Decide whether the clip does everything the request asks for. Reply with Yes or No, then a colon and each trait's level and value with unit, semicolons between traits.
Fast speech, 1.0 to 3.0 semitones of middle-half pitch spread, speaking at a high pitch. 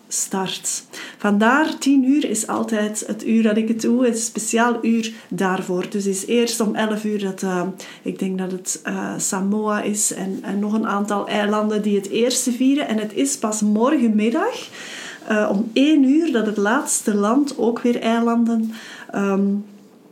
No: average, 180 wpm; narrow, 2.5 semitones; high, 220 Hz